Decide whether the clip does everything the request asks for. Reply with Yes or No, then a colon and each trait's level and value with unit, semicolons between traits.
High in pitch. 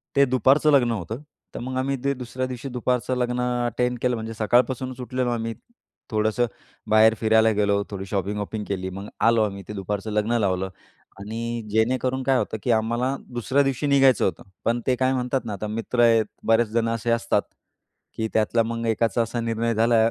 No: low, 115 Hz